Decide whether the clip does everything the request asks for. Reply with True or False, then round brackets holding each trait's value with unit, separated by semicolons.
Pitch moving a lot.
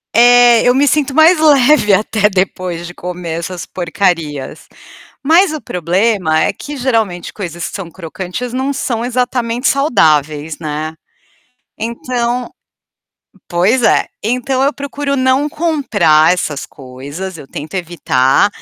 True (7.4 semitones)